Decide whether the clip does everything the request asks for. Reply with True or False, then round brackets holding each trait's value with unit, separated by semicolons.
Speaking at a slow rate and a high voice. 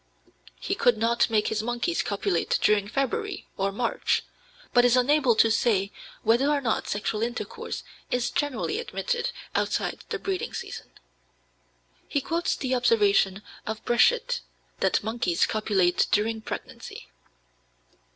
True (130 wpm; 235 Hz)